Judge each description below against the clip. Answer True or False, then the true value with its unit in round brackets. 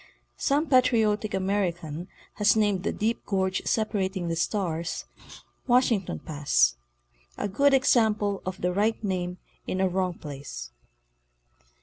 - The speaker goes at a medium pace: False (120 wpm)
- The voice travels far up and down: False (3.3 semitones)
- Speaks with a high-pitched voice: True (195 Hz)